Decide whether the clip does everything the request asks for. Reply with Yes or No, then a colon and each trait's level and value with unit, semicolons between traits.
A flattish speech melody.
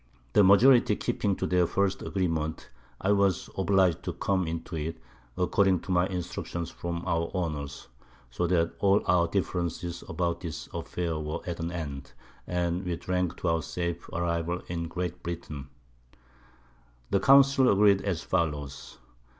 Yes: narrow, 2.3 semitones